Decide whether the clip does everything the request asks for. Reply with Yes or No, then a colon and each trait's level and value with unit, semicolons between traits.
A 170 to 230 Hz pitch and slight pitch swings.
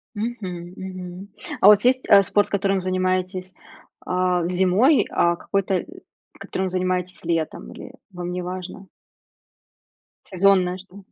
Yes: medium, 185 Hz; narrow, 1.6 semitones